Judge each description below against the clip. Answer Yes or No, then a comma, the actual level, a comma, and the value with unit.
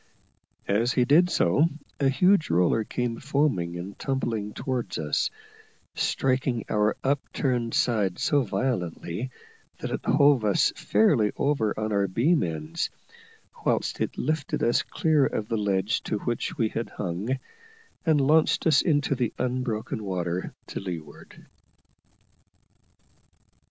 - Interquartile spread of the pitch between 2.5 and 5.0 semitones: No, wide, 5.4 semitones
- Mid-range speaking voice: No, low, 115 Hz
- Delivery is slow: Yes, slow, 130 wpm